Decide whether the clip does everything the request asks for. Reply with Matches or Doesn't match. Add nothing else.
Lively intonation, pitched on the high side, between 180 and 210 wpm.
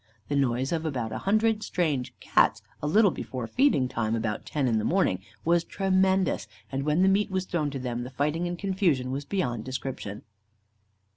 Doesn't match